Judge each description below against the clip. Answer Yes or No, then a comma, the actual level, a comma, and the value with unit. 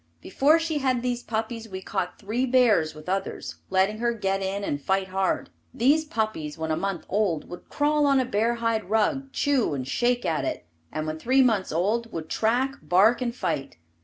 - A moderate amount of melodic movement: Yes, average, 4.9 semitones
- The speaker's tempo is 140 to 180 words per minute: No, average, 195 wpm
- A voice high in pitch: Yes, high, 220 Hz